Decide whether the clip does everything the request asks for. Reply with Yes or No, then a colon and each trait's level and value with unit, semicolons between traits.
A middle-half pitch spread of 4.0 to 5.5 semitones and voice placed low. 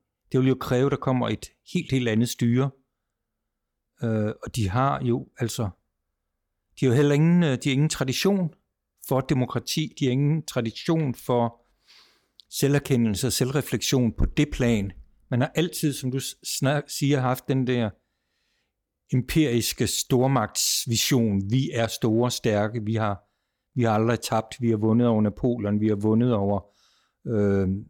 No: average, 3.6 semitones; low, 120 Hz